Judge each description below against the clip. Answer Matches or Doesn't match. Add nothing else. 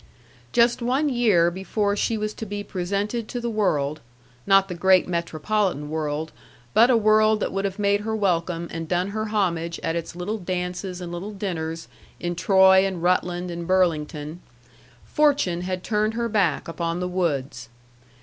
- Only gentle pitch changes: Doesn't match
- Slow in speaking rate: Doesn't match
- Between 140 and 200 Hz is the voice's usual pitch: Matches